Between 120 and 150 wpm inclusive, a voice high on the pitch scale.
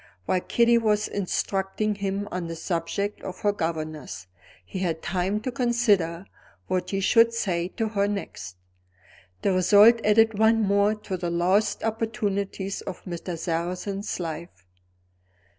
Yes: average, 140 wpm; high, 195 Hz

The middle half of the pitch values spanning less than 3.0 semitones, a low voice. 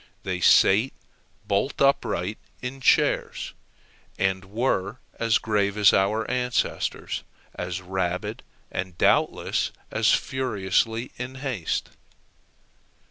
No: average, 4.7 semitones; low, 105 Hz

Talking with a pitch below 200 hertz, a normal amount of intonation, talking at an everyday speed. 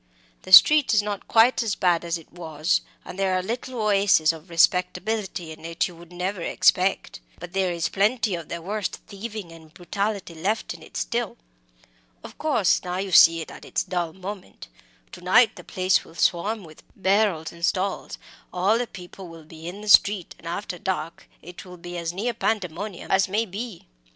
Yes: medium, 185 Hz; average, 3.3 semitones; average, 190 wpm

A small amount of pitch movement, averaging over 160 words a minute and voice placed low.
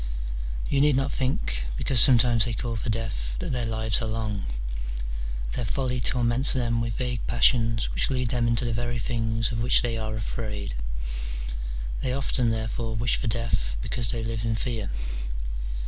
Yes: narrow, 1.8 semitones; average, 175 wpm; low, 115 Hz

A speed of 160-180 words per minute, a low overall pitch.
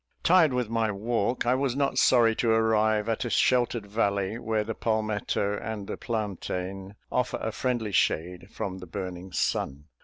Yes: average, 165 wpm; low, 110 Hz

